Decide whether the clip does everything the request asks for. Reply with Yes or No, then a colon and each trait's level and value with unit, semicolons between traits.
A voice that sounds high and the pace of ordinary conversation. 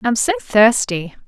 Yes: high, 220 Hz; average, 190 wpm